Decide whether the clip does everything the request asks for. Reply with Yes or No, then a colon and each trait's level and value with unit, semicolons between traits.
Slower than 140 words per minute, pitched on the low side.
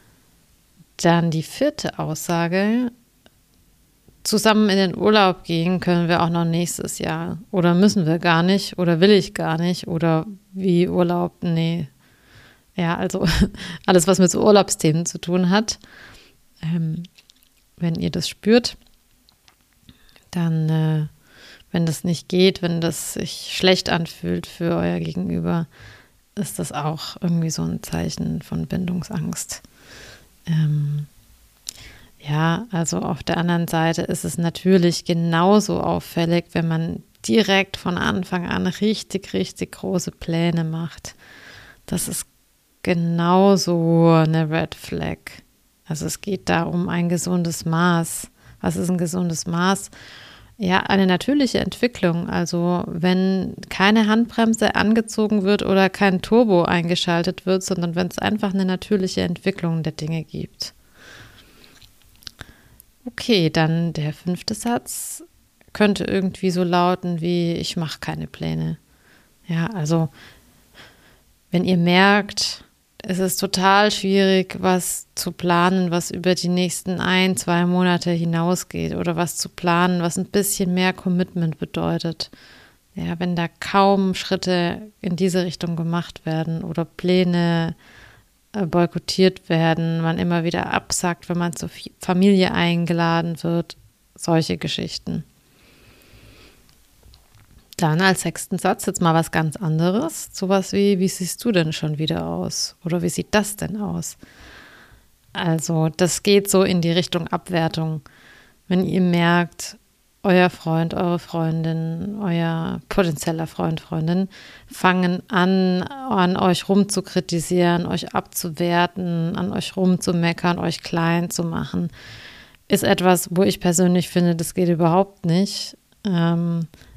No: average, 130 wpm; medium, 175 Hz